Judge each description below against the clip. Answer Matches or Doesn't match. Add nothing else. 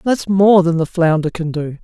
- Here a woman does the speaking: Doesn't match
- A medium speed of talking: Doesn't match